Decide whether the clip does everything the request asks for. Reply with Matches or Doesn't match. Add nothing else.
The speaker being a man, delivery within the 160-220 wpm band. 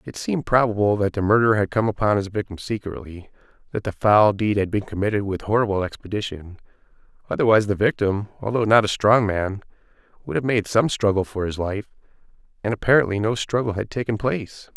Matches